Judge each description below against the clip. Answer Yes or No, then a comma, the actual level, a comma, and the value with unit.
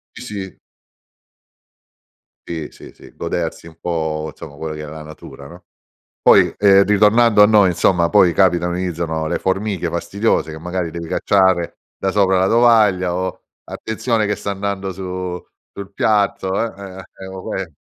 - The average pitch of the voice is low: Yes, very low, 95 Hz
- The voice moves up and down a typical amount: Yes, average, 3.1 semitones